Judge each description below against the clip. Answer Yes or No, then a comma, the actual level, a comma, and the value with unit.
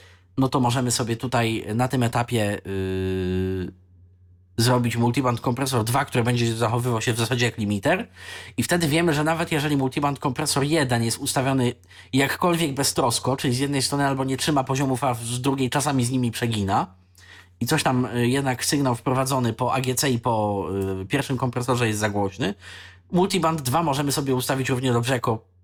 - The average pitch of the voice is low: Yes, low, 125 Hz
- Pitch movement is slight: No, average, 3.9 semitones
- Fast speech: Yes, fast, 170 wpm